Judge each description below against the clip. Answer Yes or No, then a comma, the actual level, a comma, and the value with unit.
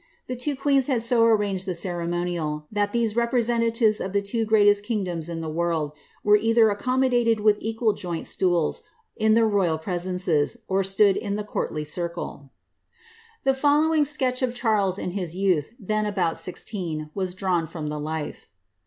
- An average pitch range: Yes, average, 4.8 semitones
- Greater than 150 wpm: Yes, average, 165 wpm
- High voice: Yes, high, 205 Hz